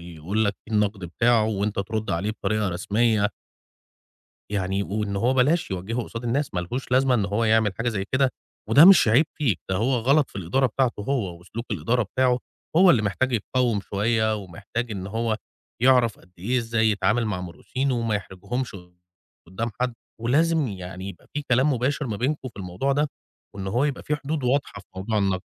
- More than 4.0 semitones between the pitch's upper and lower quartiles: Yes, average, 4.4 semitones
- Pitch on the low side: Yes, low, 110 Hz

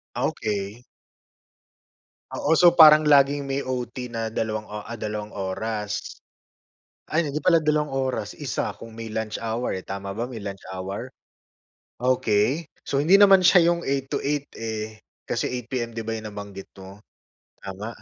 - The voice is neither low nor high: No, low, 115 Hz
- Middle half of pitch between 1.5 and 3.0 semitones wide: No, average, 5.0 semitones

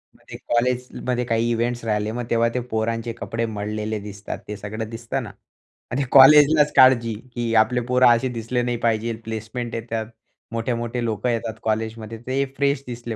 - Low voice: Yes, low, 115 Hz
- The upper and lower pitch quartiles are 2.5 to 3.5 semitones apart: No, narrow, 1.8 semitones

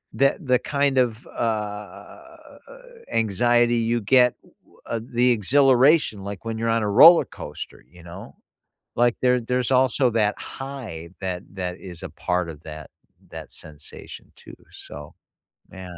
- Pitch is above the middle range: No, low, 115 Hz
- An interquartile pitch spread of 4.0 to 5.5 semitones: Yes, average, 5.1 semitones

